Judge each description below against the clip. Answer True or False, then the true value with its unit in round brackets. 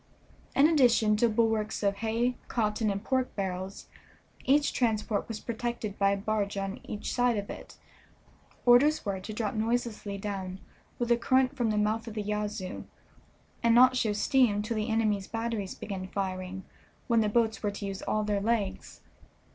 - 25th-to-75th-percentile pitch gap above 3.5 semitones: False (2.7 semitones)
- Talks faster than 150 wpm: True (170 wpm)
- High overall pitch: True (215 Hz)